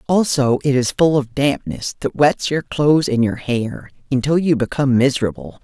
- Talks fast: No, average, 180 wpm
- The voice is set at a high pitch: No, medium, 140 Hz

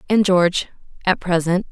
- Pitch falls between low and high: Yes, medium, 180 Hz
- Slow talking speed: Yes, slow, 105 wpm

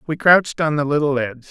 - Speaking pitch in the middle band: Yes, medium, 145 Hz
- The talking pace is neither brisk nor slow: No, fast, 240 wpm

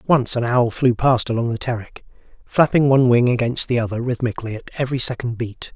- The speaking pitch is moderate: No, low, 120 Hz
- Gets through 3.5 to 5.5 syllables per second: No, 6.2 syllables/s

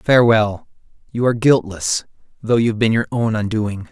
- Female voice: No, male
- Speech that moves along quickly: No, average, 155 wpm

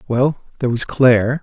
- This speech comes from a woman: No, male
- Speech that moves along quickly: No, average, 170 wpm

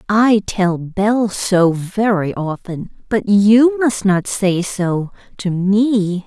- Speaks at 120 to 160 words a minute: Yes, slow, 135 wpm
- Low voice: No, high, 200 Hz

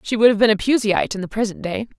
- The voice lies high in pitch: Yes, high, 215 Hz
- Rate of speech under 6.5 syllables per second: No, 7.2 syllables/s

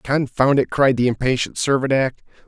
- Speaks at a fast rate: No, average, 145 wpm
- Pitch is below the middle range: Yes, low, 130 Hz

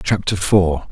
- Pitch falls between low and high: No, very low, 90 Hz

